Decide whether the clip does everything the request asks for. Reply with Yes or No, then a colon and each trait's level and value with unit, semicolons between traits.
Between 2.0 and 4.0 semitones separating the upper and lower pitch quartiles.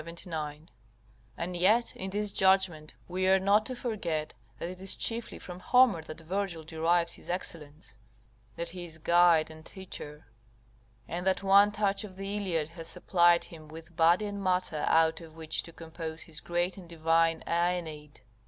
Yes: average, 2.9 semitones